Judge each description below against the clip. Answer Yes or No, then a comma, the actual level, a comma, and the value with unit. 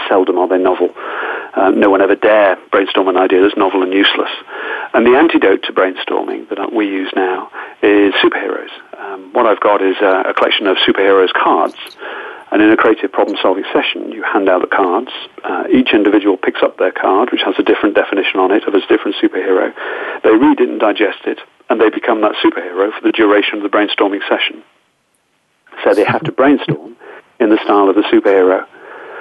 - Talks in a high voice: Yes, very high, 370 Hz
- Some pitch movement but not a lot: No, wide, 6.8 semitones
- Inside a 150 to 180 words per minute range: No, average, 195 wpm